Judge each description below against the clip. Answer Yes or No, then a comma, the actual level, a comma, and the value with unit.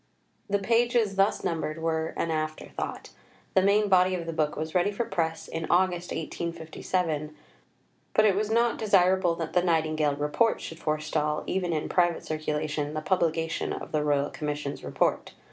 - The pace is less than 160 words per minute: No, average, 165 wpm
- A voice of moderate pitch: Yes, medium, 165 Hz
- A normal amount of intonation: Yes, average, 3.4 semitones